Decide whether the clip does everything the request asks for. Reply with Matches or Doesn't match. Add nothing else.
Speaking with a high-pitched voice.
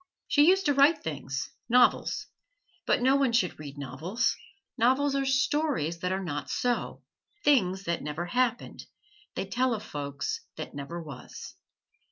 Matches